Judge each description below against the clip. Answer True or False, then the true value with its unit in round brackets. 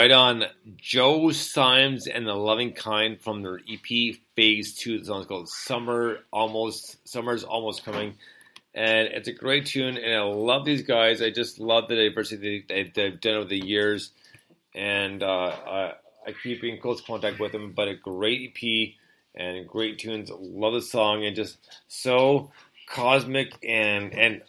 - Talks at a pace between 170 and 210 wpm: False (160 wpm)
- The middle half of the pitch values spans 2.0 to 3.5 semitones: True (2.4 semitones)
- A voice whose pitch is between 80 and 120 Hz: True (110 Hz)